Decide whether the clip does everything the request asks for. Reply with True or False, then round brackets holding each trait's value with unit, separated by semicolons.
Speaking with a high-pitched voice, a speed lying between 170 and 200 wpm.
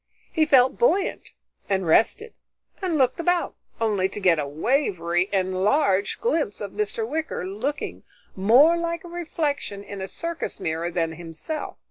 False (215 Hz; 145 wpm)